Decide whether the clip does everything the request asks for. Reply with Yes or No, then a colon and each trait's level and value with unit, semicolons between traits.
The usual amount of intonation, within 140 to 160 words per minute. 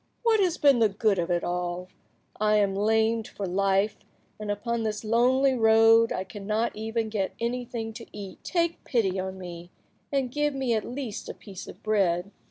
No: average, 3.3 semitones; average, 180 wpm